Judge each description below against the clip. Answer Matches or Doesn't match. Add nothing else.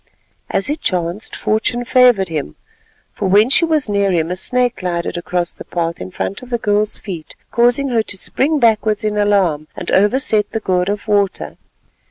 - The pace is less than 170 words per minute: Doesn't match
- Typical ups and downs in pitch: Matches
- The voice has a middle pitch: Doesn't match